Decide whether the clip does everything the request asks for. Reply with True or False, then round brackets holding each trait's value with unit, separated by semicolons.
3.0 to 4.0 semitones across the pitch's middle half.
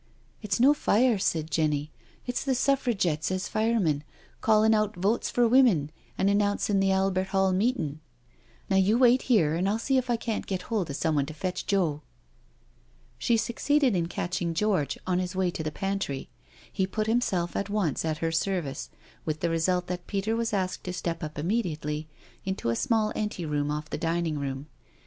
False (5.2 semitones)